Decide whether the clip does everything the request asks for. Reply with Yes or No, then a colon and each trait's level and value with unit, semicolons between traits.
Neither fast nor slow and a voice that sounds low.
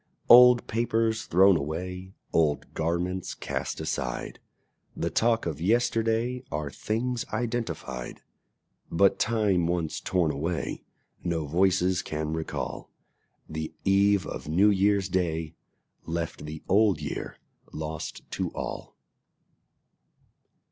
No: slow, 105 wpm; very low, 90 Hz